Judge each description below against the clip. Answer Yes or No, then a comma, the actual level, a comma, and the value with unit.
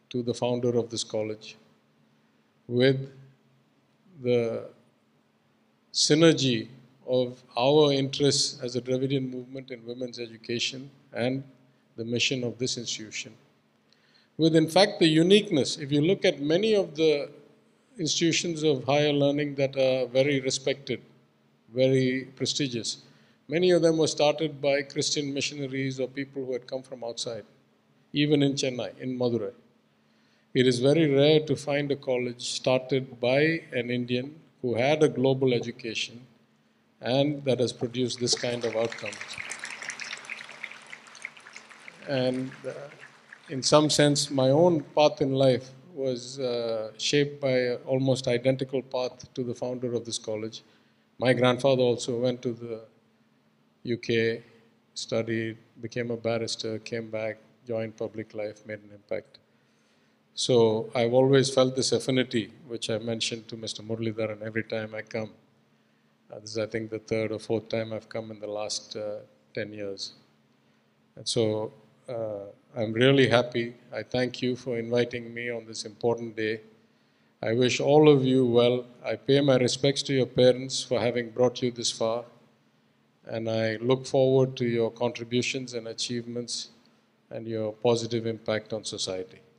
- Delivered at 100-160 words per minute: Yes, average, 145 wpm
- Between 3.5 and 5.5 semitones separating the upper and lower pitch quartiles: No, average, 3.0 semitones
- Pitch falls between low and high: No, low, 125 Hz